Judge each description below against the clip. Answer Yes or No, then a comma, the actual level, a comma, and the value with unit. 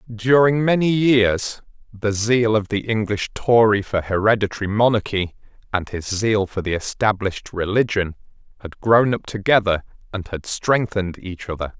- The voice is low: Yes, low, 105 Hz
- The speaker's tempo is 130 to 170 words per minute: Yes, average, 140 wpm